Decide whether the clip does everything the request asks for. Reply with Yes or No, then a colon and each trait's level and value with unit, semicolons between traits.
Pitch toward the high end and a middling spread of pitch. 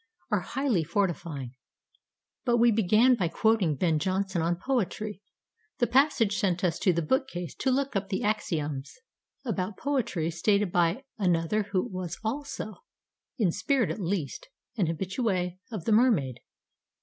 Yes: high, 195 Hz; average, 4.9 semitones